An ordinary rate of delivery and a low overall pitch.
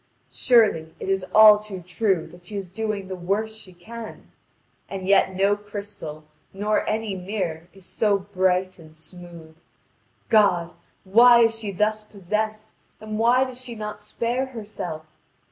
No: average, 150 wpm; high, 205 Hz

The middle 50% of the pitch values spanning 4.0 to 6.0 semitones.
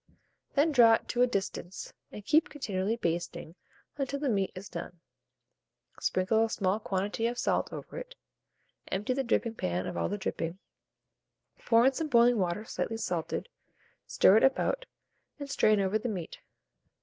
Yes: average, 4.9 semitones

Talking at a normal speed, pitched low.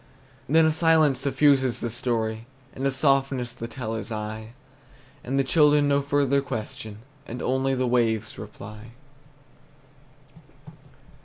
No: slow, 125 wpm; low, 130 Hz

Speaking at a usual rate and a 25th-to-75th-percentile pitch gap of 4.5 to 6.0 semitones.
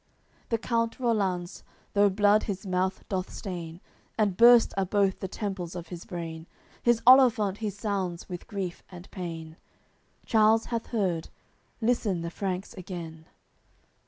No: average, 150 wpm; average, 3.6 semitones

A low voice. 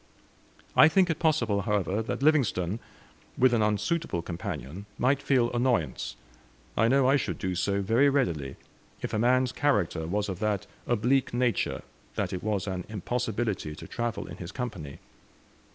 Yes: low, 110 Hz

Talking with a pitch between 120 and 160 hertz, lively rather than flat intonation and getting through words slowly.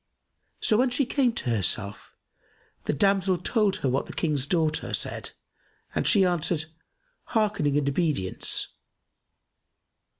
No: medium, 170 Hz; wide, 6.8 semitones; slow, 125 wpm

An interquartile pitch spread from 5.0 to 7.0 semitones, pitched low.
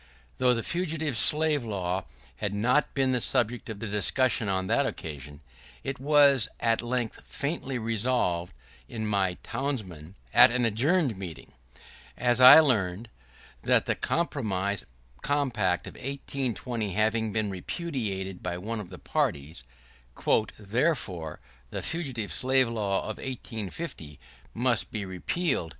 Yes: average, 5.3 semitones; low, 115 Hz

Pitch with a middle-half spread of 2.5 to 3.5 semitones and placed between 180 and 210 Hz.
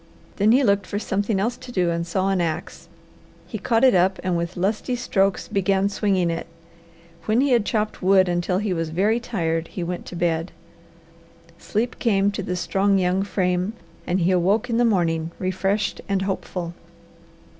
Yes: average, 2.9 semitones; high, 190 Hz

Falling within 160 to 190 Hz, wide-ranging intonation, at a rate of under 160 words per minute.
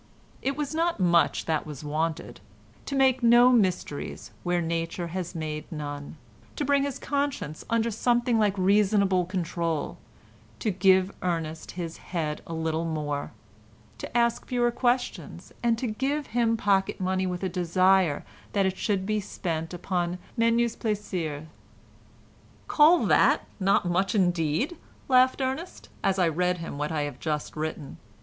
Yes: medium, 185 Hz; wide, 6.1 semitones; average, 150 wpm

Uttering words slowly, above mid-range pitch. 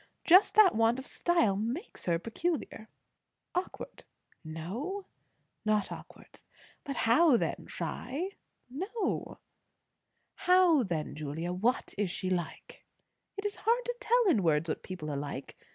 Yes: slow, 130 wpm; high, 235 Hz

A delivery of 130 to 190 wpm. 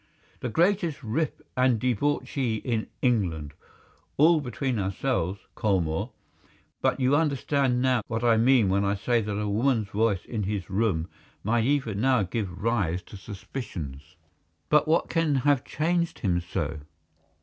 Yes: average, 145 wpm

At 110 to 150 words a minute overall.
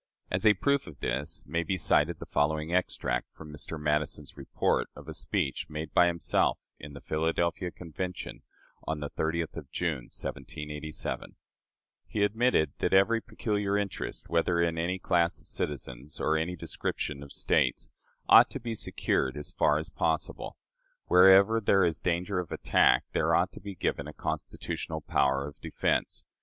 No: average, 165 wpm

